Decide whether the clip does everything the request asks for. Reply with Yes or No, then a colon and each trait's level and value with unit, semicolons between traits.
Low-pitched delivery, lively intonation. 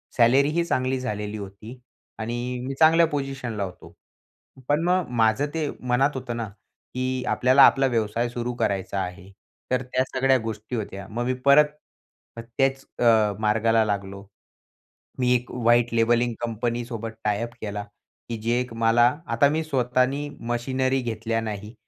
No: low, 120 Hz; average, 2.9 semitones